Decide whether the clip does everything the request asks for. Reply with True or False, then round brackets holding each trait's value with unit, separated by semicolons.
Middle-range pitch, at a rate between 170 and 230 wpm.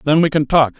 False (150 Hz; 300 wpm)